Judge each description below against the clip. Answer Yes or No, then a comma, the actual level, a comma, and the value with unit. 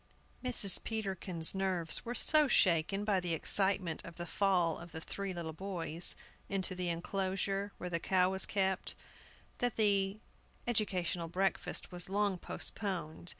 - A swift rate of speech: No, average, 145 wpm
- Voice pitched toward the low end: No, high, 190 Hz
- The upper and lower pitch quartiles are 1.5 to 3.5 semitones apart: Yes, narrow, 2.5 semitones